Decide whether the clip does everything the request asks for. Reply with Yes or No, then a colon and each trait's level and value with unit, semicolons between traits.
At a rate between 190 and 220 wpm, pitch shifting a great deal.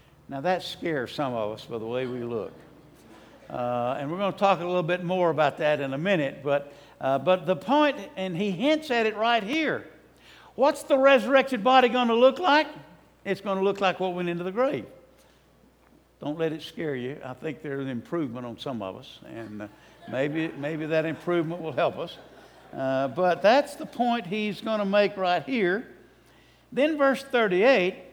Yes: average, 200 wpm; wide, 8.6 semitones